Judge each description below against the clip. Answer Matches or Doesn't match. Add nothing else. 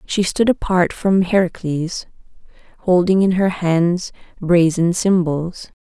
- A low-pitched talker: Doesn't match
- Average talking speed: Doesn't match